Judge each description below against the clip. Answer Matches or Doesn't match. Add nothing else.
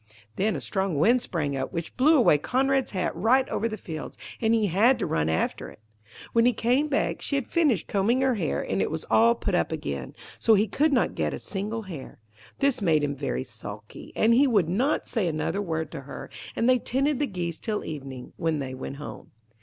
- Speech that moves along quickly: Matches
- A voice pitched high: Matches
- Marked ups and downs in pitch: Matches